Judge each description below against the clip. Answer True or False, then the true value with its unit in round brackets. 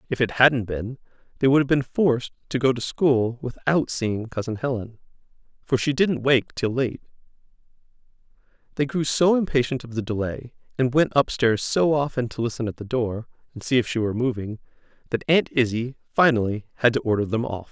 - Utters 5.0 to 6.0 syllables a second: True (5.4 syllables/s)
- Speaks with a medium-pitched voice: False (125 Hz)